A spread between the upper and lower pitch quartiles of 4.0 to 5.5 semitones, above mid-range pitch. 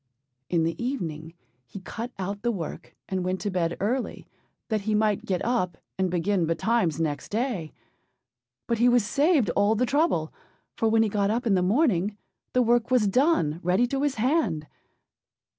Yes: average, 5.2 semitones; high, 210 Hz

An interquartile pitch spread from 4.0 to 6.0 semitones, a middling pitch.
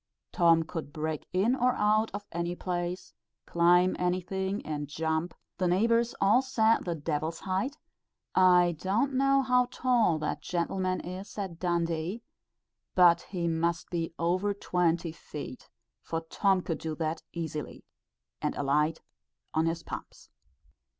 No: average, 3.5 semitones; medium, 175 Hz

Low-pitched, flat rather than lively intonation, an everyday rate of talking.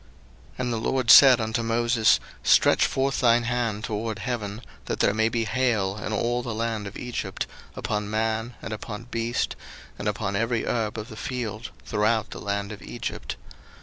Yes: low, 115 Hz; narrow, 2.0 semitones; average, 180 wpm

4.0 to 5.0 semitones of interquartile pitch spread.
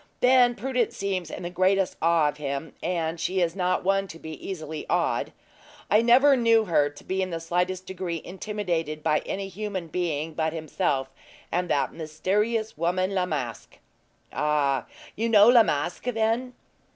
Yes: average, 4.5 semitones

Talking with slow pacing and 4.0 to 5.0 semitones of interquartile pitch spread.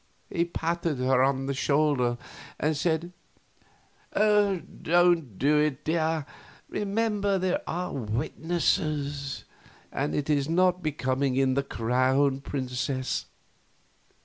Yes: slow, 105 wpm; average, 4.4 semitones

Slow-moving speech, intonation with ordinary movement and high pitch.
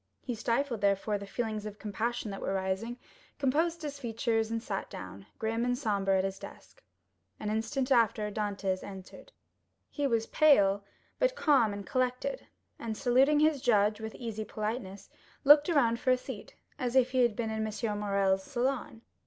No: average, 170 wpm; average, 3.9 semitones; high, 225 Hz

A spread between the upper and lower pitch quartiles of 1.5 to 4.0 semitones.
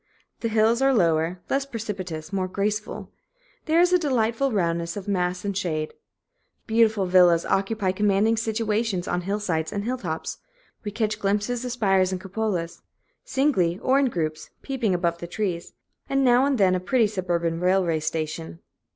No: average, 4.4 semitones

